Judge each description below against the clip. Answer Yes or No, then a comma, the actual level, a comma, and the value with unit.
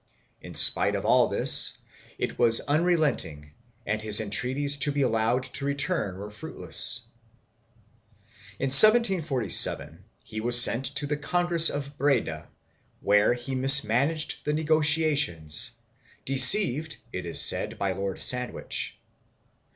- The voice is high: No, low, 135 Hz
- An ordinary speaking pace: No, slow, 130 wpm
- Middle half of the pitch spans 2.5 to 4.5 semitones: No, wide, 5.5 semitones